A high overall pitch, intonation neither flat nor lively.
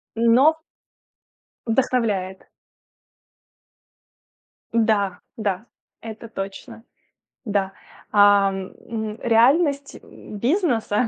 Yes: high, 225 Hz; average, 3.2 semitones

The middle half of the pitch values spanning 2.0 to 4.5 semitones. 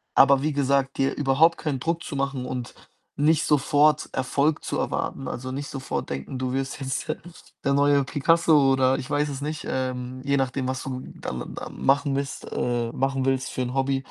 No: narrow, 1.6 semitones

